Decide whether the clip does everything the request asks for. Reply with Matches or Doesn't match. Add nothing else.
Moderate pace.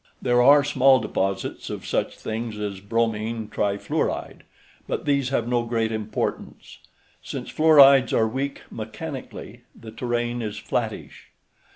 Doesn't match